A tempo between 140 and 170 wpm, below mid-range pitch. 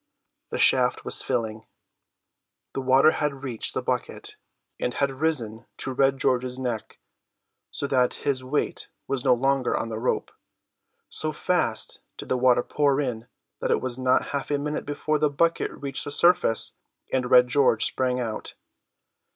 Yes: average, 160 wpm; low, 130 Hz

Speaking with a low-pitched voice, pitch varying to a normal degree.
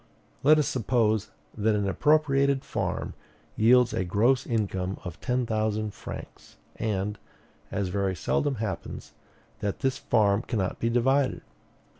Yes: low, 110 Hz; average, 4.3 semitones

